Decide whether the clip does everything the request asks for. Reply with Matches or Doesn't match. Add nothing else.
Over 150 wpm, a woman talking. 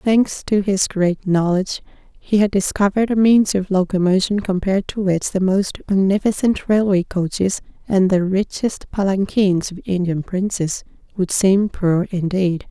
Doesn't match